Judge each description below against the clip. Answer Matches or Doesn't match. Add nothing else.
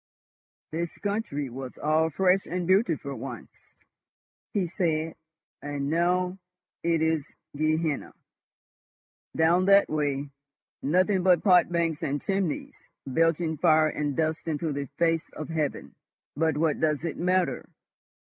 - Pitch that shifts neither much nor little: Matches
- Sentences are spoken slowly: Matches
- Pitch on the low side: Doesn't match